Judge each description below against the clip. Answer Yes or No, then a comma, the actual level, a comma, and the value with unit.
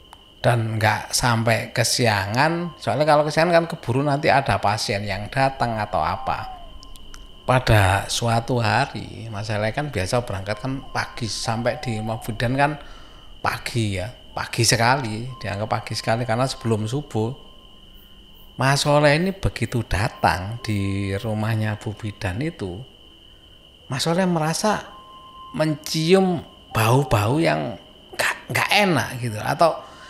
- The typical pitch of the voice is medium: No, low, 115 Hz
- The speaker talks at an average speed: Yes, average, 120 wpm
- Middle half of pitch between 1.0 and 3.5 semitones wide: No, average, 4.7 semitones